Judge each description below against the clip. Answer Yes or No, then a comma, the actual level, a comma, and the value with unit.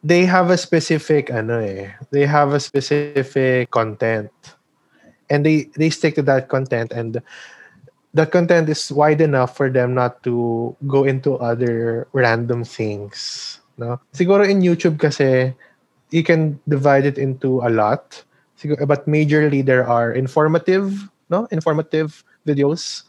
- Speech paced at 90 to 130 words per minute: No, average, 140 wpm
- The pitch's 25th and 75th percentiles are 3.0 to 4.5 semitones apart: Yes, average, 4.1 semitones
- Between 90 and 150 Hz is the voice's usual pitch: Yes, medium, 140 Hz